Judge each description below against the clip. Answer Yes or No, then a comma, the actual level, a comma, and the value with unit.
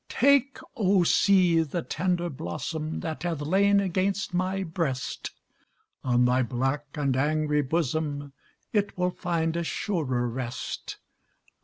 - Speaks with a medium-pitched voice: Yes, medium, 160 Hz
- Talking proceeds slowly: Yes, slow, 125 wpm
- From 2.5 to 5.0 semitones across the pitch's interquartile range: Yes, average, 4.7 semitones